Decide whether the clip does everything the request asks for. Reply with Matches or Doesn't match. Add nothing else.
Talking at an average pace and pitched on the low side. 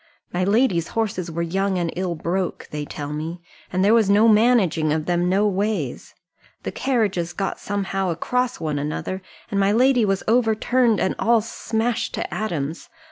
Doesn't match